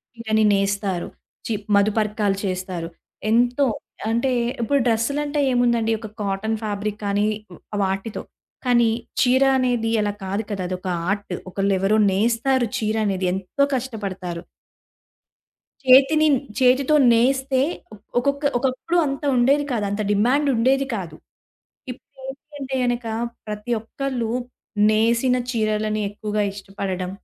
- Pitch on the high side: Yes, high, 225 Hz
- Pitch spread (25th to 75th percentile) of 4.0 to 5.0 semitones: Yes, average, 4.3 semitones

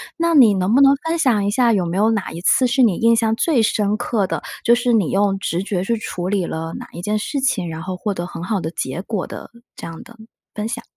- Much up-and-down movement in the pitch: No, average, 4.3 semitones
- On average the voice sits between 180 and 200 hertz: No, high, 210 Hz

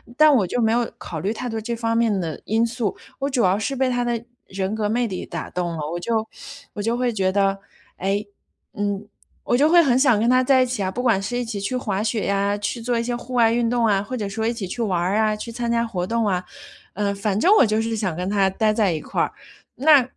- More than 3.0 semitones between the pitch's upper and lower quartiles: Yes, average, 3.4 semitones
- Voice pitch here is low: No, high, 220 Hz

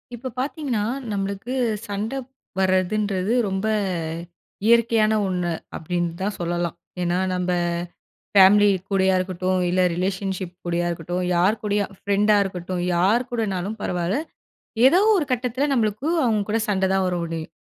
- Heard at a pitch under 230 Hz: Yes, high, 195 Hz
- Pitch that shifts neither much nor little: Yes, average, 3.1 semitones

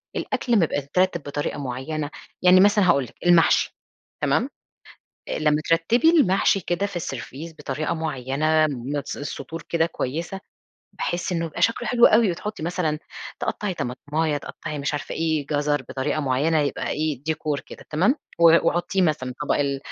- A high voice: No, medium, 155 Hz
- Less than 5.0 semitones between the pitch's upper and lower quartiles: Yes, average, 3.5 semitones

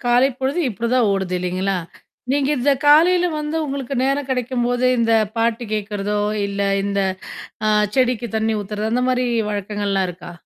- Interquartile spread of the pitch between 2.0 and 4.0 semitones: No, average, 4.4 semitones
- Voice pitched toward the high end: Yes, high, 235 Hz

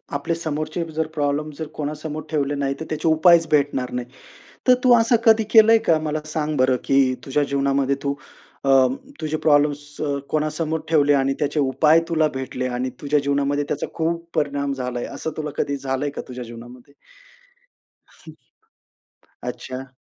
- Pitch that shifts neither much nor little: No, narrow, 2.3 semitones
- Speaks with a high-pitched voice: No, medium, 145 Hz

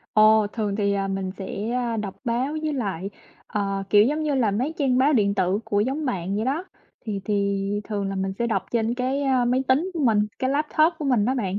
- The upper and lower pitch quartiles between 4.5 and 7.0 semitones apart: Yes, average, 4.8 semitones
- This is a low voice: No, high, 225 Hz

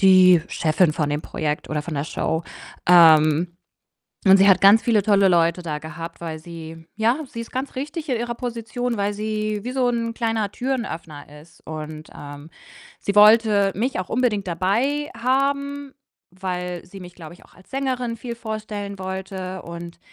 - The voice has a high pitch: Yes, high, 195 Hz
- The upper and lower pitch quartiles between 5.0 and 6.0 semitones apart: Yes, wide, 5.5 semitones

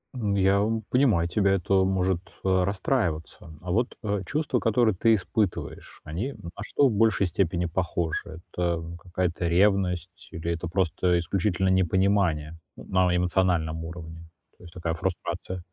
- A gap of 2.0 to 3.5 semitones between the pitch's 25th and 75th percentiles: Yes, average, 2.7 semitones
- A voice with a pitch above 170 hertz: No, very low, 90 Hz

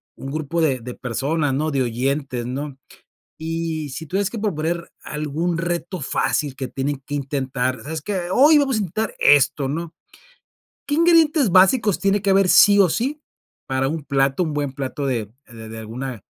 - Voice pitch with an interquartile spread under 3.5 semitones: No, wide, 5.4 semitones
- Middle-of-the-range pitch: Yes, medium, 150 Hz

